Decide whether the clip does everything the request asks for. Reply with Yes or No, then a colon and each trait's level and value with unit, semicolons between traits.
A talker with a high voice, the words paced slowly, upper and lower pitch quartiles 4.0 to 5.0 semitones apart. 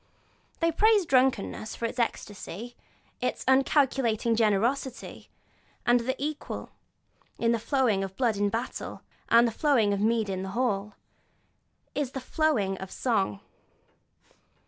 Yes: high, 235 Hz; slow, 125 wpm; average, 4.4 semitones